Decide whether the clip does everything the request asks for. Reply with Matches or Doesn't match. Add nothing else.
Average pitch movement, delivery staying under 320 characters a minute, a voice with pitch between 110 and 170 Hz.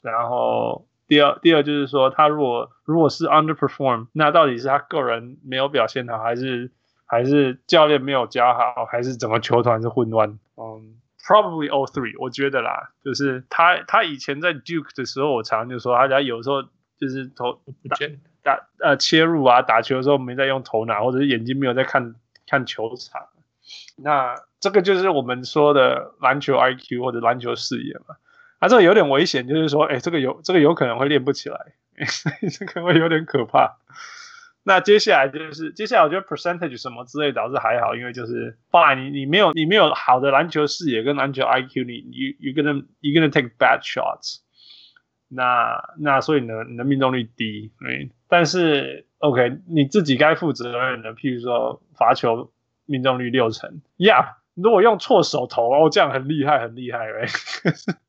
Doesn't match